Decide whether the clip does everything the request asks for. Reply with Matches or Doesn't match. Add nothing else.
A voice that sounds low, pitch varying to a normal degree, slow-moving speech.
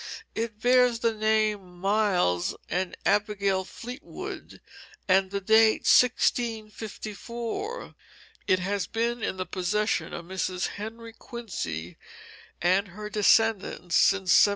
Doesn't match